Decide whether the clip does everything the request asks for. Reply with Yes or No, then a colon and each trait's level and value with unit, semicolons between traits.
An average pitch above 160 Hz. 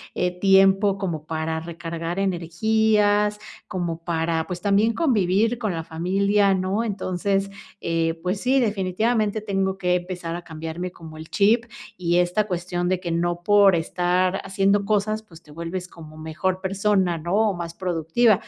Yes: medium, 185 Hz